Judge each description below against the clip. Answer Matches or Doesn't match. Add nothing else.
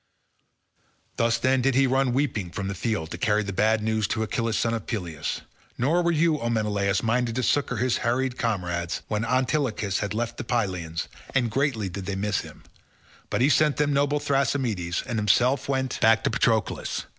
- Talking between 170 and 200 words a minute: Matches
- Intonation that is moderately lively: Matches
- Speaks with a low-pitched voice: Matches